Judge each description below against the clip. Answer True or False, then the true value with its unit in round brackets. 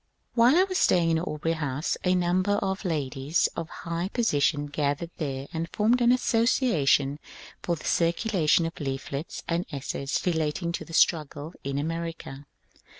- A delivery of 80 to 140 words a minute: False (150 wpm)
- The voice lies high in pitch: False (165 Hz)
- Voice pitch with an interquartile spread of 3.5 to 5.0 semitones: True (3.9 semitones)